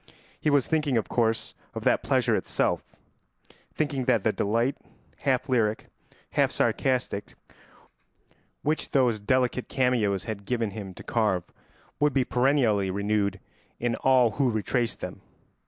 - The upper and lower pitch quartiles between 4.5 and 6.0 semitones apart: No, average, 3.7 semitones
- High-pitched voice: No, low, 120 Hz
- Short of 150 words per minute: Yes, slow, 135 wpm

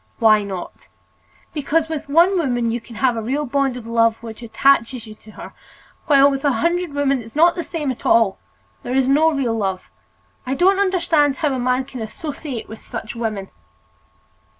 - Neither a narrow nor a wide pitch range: Yes, average, 4.6 semitones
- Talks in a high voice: Yes, very high, 265 Hz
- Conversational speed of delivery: Yes, average, 185 wpm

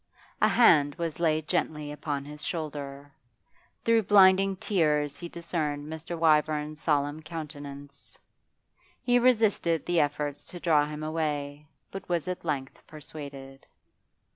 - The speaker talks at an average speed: No, slow, 125 wpm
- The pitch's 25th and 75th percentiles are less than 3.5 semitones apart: Yes, average, 2.8 semitones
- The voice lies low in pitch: No, medium, 155 Hz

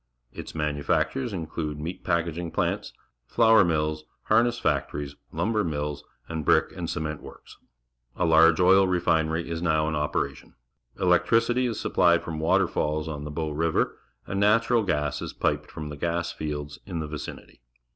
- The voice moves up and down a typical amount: Yes, average, 3.4 semitones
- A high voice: No, very low, 80 Hz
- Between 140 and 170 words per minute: Yes, average, 155 wpm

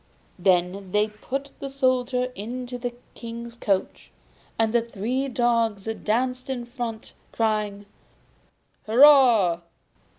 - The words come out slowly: Yes, slow, 105 wpm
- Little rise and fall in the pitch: No, average, 3.1 semitones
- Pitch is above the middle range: Yes, high, 235 Hz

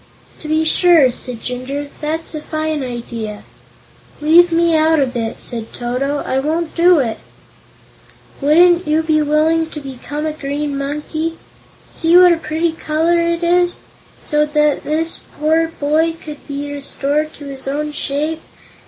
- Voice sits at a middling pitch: No, very high, 305 Hz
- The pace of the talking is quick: No, average, 155 wpm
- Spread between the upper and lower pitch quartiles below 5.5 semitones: Yes, narrow, 2.5 semitones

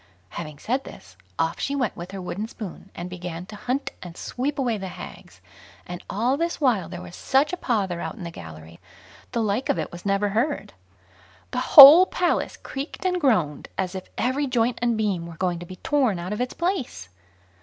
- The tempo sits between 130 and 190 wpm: No, fast, 205 wpm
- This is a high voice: Yes, high, 210 Hz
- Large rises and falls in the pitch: Yes, wide, 6.8 semitones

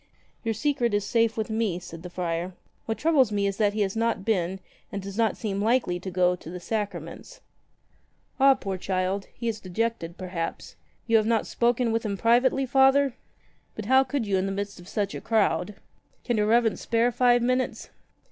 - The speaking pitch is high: Yes, high, 215 Hz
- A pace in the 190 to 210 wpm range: Yes, average, 200 wpm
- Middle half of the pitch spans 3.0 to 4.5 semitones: Yes, average, 3.5 semitones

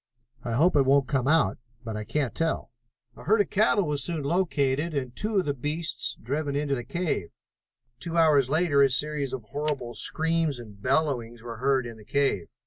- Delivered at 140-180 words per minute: No, average, 195 wpm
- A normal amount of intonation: Yes, average, 4.3 semitones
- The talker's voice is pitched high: No, medium, 140 Hz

